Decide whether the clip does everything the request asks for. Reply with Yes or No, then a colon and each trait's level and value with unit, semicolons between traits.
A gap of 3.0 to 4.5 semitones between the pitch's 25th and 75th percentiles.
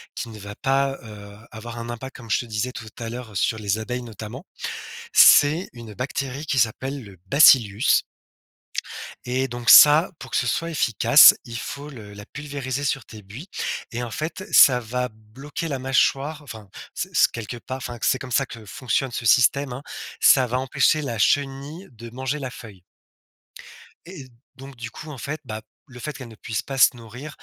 Yes: average, 3.4 semitones